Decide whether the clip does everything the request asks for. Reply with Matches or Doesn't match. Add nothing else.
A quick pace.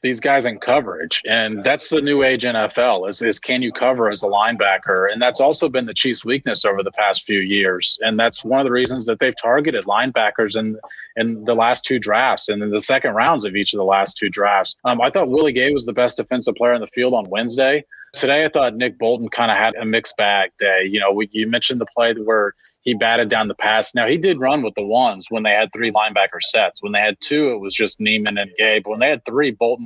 Matches